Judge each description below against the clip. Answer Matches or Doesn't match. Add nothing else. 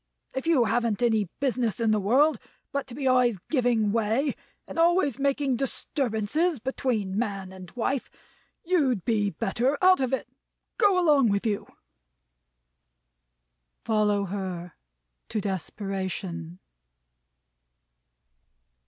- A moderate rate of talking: Doesn't match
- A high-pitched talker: Matches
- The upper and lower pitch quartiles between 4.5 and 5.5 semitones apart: Matches